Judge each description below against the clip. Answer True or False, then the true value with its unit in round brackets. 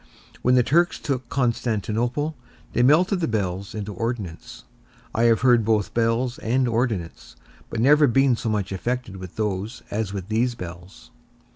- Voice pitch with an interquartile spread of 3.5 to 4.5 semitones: True (4.0 semitones)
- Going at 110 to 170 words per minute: True (155 wpm)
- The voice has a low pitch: True (115 Hz)